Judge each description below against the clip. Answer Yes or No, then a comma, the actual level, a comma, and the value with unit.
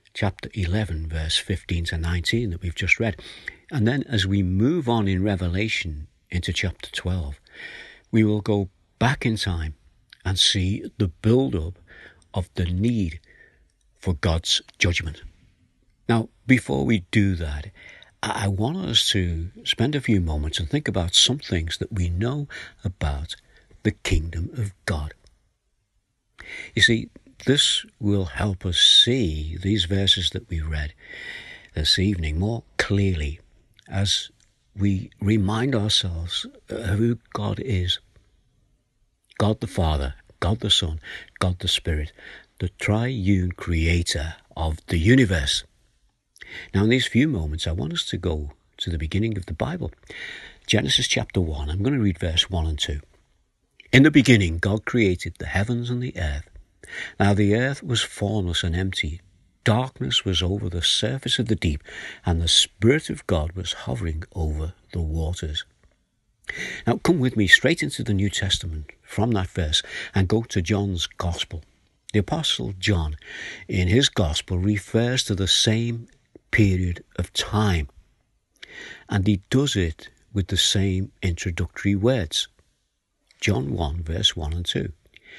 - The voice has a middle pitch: No, very low, 95 Hz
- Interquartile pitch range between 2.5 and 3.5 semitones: No, average, 4.0 semitones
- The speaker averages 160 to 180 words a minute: No, average, 150 wpm